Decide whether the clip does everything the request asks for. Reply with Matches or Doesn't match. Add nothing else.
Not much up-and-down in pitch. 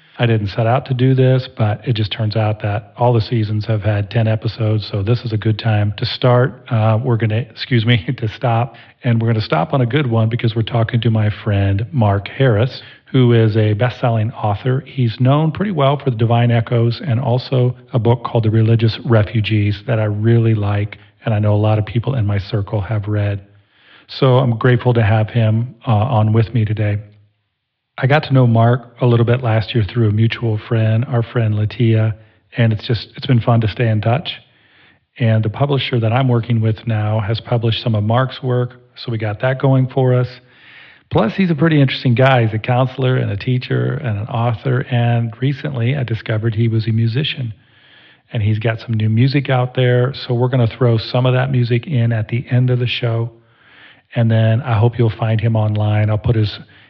Matches